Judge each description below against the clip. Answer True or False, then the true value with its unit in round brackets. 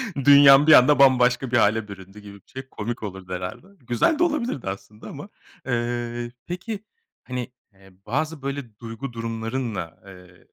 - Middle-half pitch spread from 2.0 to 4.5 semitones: False (4.9 semitones)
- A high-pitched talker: False (120 Hz)